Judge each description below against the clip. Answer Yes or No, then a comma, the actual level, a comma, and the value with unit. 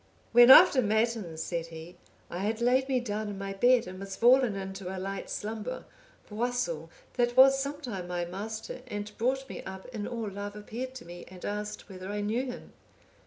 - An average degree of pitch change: Yes, average, 4.2 semitones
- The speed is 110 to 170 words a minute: No, average, 190 wpm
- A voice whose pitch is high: Yes, high, 210 Hz